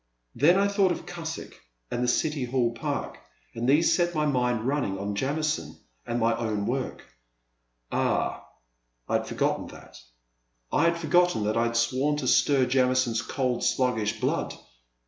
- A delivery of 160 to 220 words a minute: Yes, average, 165 wpm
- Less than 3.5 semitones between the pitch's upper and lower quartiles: No, average, 4.7 semitones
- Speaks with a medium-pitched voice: No, low, 125 Hz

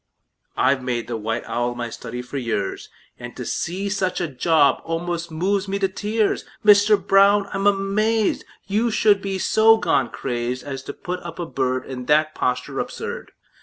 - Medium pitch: Yes, medium, 170 Hz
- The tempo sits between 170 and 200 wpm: Yes, average, 175 wpm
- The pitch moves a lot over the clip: Yes, wide, 7.7 semitones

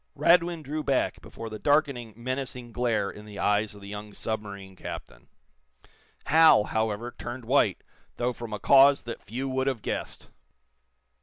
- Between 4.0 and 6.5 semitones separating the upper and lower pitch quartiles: Yes, average, 4.3 semitones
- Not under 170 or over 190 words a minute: No, average, 155 wpm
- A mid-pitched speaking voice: No, low, 120 Hz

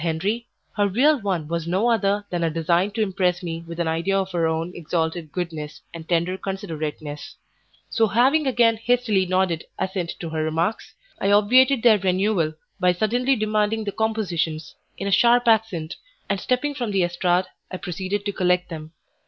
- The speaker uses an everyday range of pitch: Yes, average, 4.5 semitones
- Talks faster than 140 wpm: Yes, average, 175 wpm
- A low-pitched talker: No, high, 190 Hz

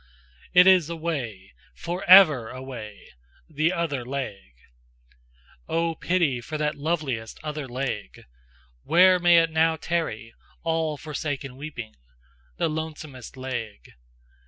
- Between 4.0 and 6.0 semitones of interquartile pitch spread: Yes, average, 4.7 semitones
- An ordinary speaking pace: No, slow, 115 wpm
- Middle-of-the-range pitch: Yes, medium, 150 Hz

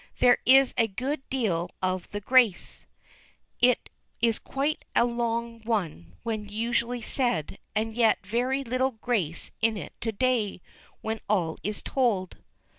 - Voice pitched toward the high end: Yes, high, 230 Hz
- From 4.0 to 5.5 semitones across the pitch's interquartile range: No, average, 3.3 semitones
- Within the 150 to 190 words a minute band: No, average, 140 wpm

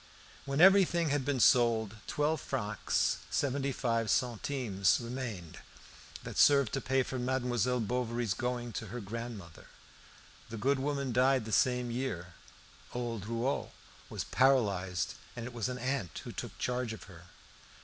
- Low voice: Yes, low, 125 Hz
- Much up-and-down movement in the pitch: No, average, 3.1 semitones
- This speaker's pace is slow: No, average, 145 wpm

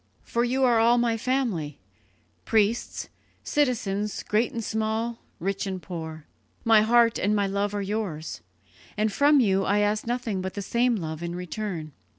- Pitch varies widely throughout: No, average, 3.5 semitones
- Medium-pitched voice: No, high, 210 Hz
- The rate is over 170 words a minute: No, average, 165 wpm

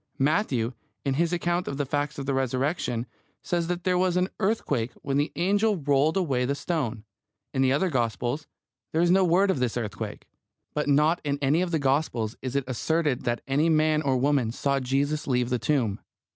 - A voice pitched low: No, medium, 145 Hz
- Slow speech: No, average, 200 wpm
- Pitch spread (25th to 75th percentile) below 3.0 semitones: No, average, 4.5 semitones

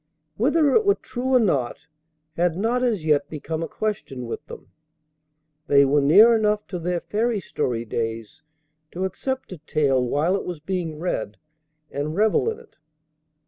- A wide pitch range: Yes, wide, 7.3 semitones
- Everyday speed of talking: Yes, average, 165 wpm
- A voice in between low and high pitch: Yes, medium, 175 Hz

